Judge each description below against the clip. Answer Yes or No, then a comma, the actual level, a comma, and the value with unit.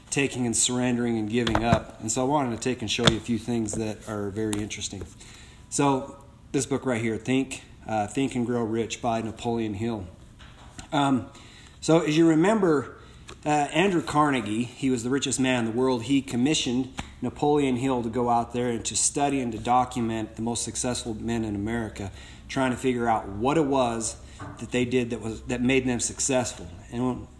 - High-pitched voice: No, low, 120 Hz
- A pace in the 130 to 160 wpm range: No, average, 195 wpm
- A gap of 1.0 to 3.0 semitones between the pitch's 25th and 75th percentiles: Yes, average, 2.7 semitones